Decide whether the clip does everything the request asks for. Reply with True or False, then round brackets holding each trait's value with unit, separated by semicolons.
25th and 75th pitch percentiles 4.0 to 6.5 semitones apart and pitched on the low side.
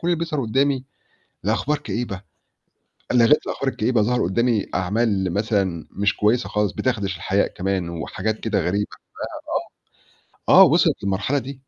True (4.4 semitones; 110 Hz)